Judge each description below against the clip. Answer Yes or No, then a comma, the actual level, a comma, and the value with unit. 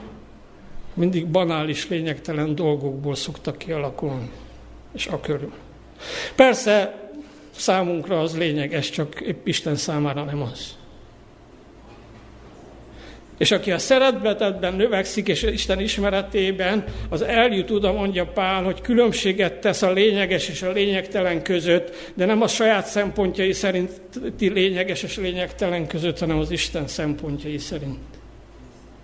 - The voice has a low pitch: No, medium, 185 Hz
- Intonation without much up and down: No, average, 3.7 semitones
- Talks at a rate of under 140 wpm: Yes, average, 120 wpm